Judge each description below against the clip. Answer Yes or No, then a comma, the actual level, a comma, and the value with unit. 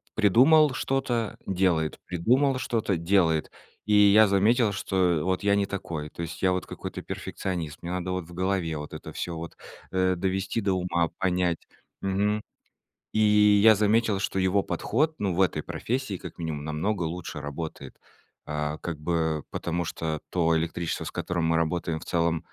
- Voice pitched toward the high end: No, very low, 90 Hz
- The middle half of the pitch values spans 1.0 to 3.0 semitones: No, average, 3.7 semitones